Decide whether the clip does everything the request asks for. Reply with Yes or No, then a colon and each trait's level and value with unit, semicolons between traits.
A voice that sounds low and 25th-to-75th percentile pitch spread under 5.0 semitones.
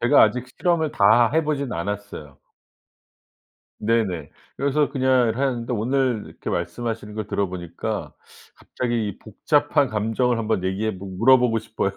Yes: low, 115 Hz; average, 4.1 semitones